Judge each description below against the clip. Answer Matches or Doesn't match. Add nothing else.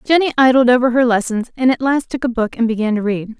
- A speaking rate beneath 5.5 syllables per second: Doesn't match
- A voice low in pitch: Doesn't match